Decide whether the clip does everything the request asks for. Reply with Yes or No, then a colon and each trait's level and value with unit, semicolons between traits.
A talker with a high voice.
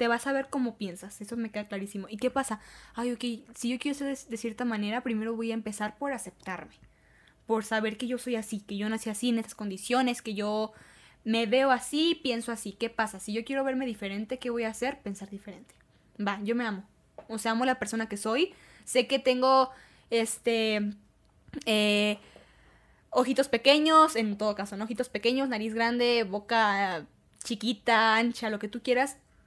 Yes: high, 230 Hz